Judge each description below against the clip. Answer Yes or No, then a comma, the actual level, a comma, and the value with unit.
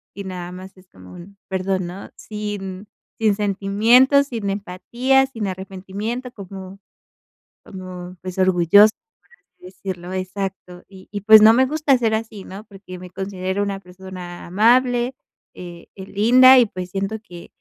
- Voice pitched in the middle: No, high, 195 Hz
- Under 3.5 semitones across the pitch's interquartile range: Yes, average, 2.8 semitones